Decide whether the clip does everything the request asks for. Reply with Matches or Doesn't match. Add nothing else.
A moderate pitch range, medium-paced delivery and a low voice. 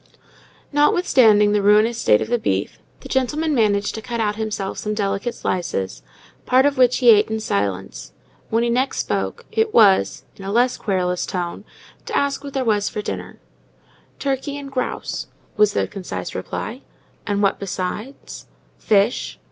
Doesn't match